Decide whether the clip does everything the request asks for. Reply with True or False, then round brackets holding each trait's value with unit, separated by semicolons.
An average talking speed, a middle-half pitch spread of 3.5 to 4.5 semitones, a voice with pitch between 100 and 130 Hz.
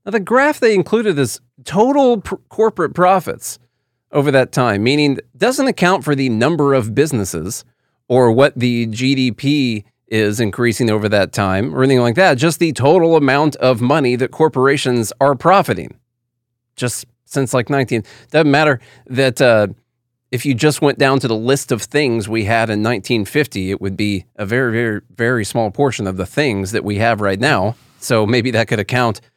True (180 wpm; 3.8 semitones; 125 Hz)